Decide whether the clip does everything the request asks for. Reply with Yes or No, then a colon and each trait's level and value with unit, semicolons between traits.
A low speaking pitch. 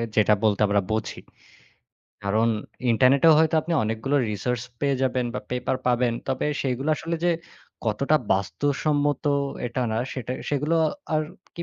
Yes: low, 130 Hz